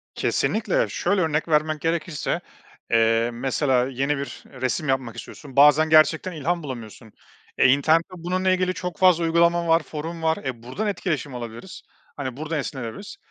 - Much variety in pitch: No, average, 4.4 semitones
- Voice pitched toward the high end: No, medium, 155 Hz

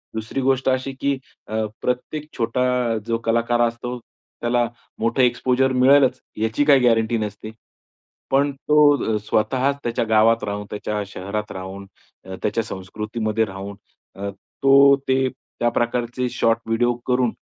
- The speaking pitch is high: No, low, 115 Hz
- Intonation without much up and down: No, average, 3.2 semitones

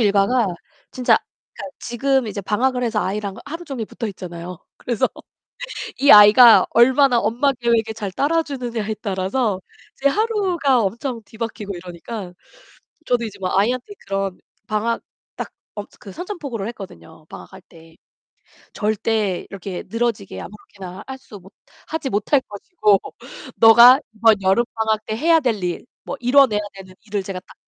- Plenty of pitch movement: No, average, 4.3 semitones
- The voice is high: Yes, high, 220 Hz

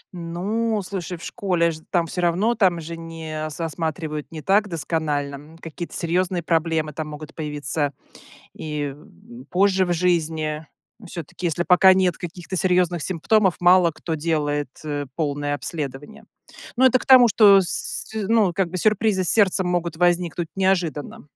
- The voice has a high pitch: No, medium, 170 Hz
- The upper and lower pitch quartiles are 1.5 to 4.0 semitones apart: Yes, average, 3.3 semitones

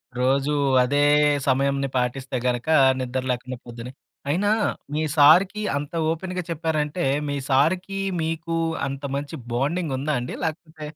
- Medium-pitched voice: Yes, medium, 145 Hz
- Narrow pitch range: No, average, 3.9 semitones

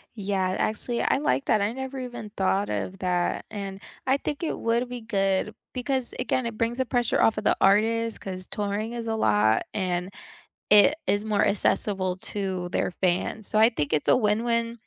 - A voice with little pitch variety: No, average, 3.5 semitones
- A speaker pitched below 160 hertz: No, high, 215 Hz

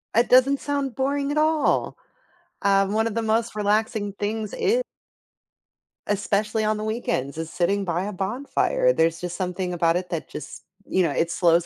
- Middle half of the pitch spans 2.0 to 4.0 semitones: No, average, 4.9 semitones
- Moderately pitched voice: No, high, 210 Hz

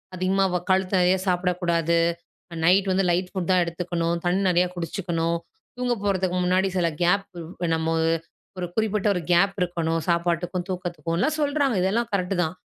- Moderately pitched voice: Yes, medium, 180 Hz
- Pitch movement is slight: Yes, narrow, 2.1 semitones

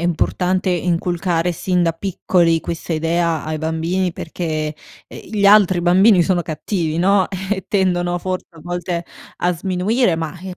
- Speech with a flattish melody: Yes, narrow, 2.0 semitones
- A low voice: No, medium, 175 Hz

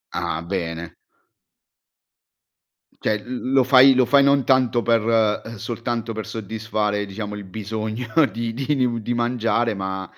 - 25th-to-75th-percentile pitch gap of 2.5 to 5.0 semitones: Yes, average, 2.8 semitones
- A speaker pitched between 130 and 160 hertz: No, low, 115 Hz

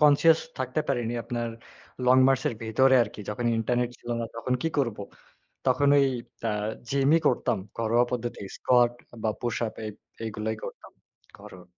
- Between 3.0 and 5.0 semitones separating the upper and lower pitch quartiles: No, narrow, 2.5 semitones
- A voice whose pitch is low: Yes, low, 120 Hz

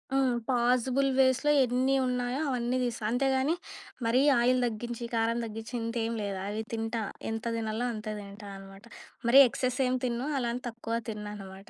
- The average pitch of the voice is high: Yes, high, 235 Hz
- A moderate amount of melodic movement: No, narrow, 2.2 semitones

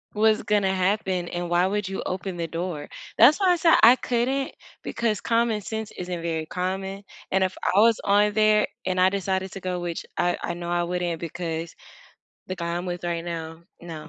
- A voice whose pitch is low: No, medium, 185 Hz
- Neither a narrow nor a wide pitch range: Yes, average, 3.2 semitones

